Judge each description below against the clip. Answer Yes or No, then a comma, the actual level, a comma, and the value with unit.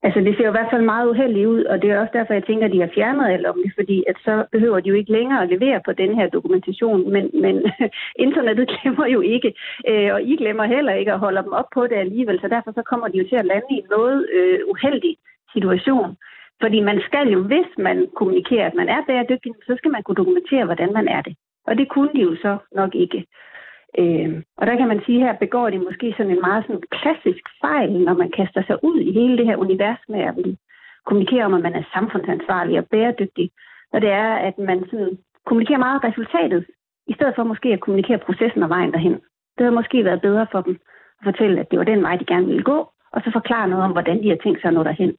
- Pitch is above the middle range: Yes, high, 220 Hz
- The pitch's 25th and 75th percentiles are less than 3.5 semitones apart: No, wide, 5.4 semitones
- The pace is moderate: No, fast, 250 wpm